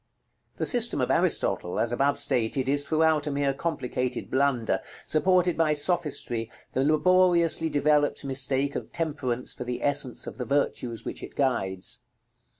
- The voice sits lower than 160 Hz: Yes, medium, 140 Hz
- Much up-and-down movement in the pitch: No, average, 3.8 semitones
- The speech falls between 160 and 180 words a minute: No, average, 150 wpm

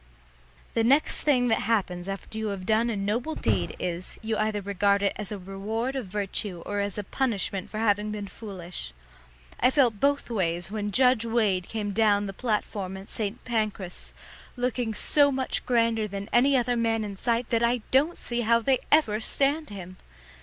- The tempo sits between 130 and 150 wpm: No, average, 185 wpm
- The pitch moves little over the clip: No, average, 3.3 semitones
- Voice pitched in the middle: No, high, 215 Hz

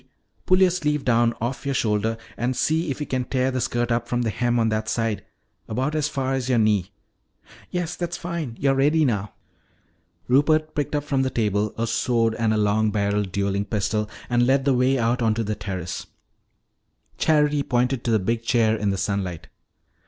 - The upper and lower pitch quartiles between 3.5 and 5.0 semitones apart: Yes, average, 4.0 semitones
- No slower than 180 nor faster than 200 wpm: Yes, average, 195 wpm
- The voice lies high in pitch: No, low, 120 Hz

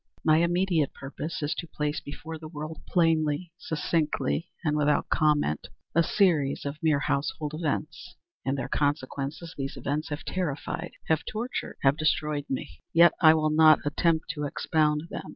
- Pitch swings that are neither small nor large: No, narrow, 1.9 semitones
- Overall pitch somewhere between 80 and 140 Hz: No, medium, 155 Hz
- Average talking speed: Yes, average, 150 wpm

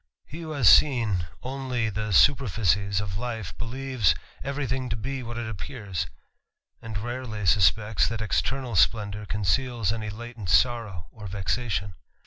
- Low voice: Yes, low, 110 Hz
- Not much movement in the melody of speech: No, average, 3.7 semitones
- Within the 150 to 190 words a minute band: No, average, 140 wpm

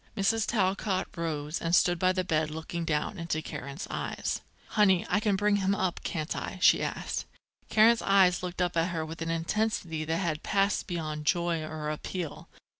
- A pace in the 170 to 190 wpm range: Yes, average, 185 wpm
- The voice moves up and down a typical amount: Yes, average, 3.4 semitones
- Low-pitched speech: No, medium, 175 Hz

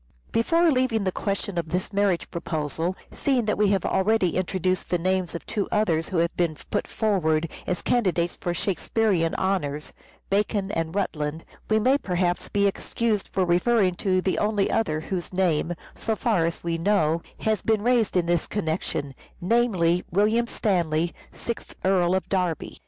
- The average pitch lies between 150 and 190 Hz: Yes, medium, 185 Hz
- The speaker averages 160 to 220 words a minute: Yes, average, 165 wpm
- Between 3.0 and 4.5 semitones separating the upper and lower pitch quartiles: Yes, average, 3.8 semitones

